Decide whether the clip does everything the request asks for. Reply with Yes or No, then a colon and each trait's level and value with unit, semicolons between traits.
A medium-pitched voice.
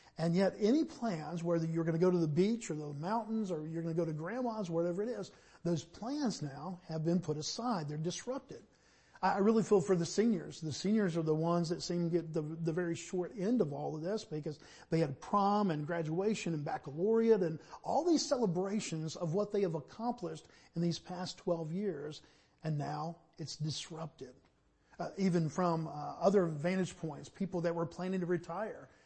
Yes: medium, 175 Hz